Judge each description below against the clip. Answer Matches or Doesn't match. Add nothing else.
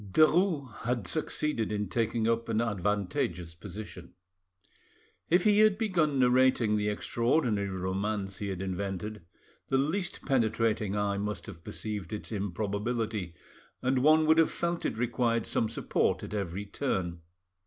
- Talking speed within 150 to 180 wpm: Doesn't match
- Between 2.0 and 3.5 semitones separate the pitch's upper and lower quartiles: Doesn't match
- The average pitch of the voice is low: Matches